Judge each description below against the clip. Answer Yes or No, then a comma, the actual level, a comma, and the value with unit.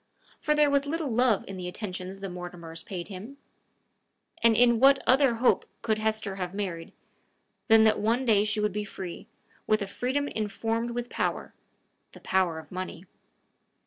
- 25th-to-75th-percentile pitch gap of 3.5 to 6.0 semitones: Yes, average, 4.3 semitones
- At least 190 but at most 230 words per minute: No, average, 170 wpm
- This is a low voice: No, high, 215 Hz